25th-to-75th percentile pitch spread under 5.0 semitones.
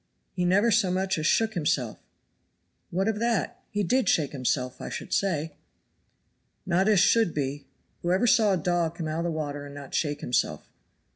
No: average, 5.3 semitones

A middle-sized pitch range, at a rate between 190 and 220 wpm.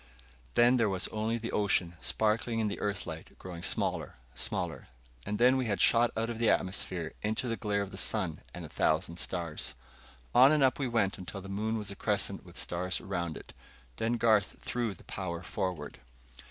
Yes: average, 4.1 semitones; average, 195 wpm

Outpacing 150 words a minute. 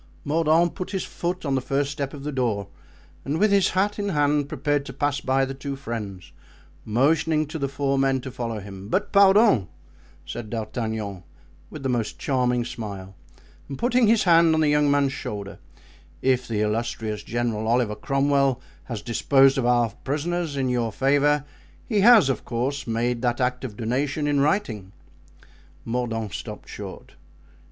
Yes: average, 170 wpm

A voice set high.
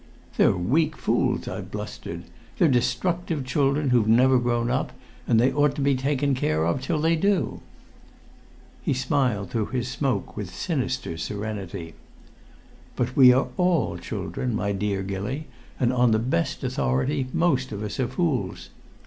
No: low, 125 Hz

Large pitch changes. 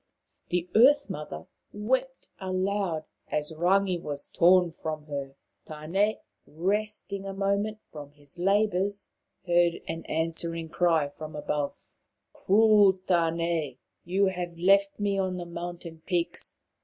No: average, 3.6 semitones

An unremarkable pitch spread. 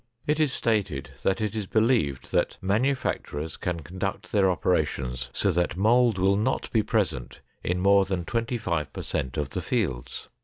No: wide, 5.8 semitones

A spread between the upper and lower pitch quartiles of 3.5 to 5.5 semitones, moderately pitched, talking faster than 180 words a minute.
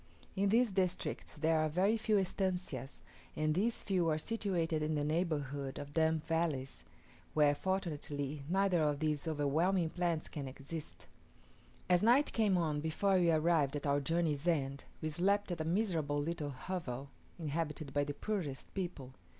No: average, 4.1 semitones; medium, 160 Hz; average, 160 wpm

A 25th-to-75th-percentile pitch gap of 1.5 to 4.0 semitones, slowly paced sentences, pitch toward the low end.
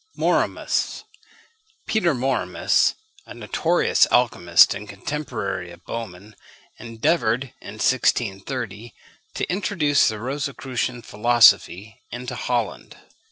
No: average, 4.6 semitones; slow, 90 wpm; low, 120 Hz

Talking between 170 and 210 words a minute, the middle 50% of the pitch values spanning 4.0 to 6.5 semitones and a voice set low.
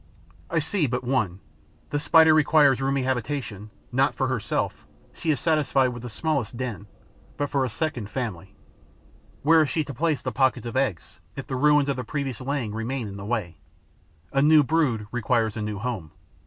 Yes: average, 190 wpm; average, 4.5 semitones; low, 130 Hz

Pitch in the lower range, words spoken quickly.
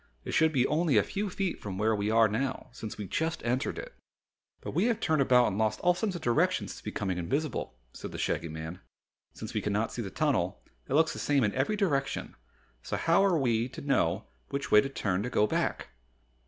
Yes: low, 130 Hz; fast, 220 wpm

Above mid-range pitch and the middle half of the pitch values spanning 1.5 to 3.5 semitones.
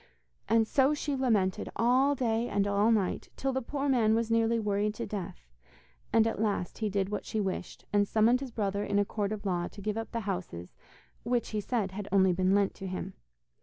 Yes: high, 210 Hz; average, 2.7 semitones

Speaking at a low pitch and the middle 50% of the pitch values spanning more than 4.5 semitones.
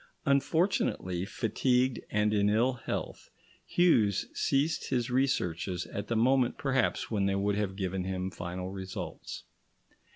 Yes: low, 105 Hz; wide, 5.4 semitones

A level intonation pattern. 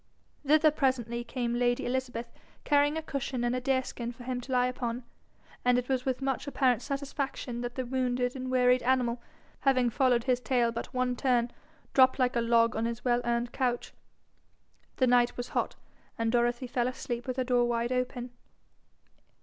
Yes: narrow, 1.3 semitones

